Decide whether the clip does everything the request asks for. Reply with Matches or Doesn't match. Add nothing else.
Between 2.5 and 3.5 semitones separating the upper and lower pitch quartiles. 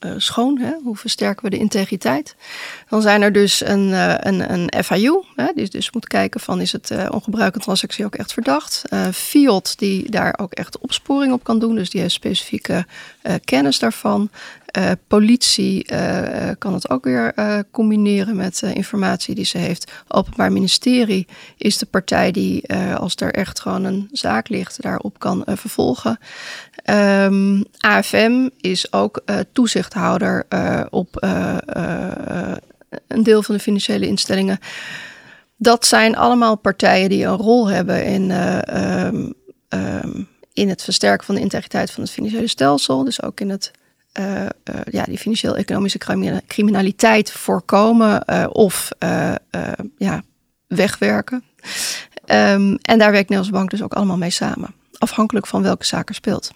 Matches